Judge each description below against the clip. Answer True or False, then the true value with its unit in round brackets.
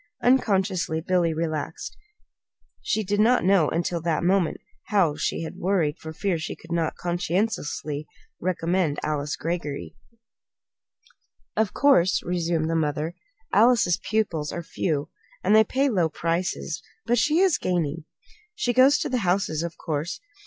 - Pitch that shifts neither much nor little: True (4.2 semitones)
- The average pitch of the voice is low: False (175 Hz)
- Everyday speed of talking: True (145 wpm)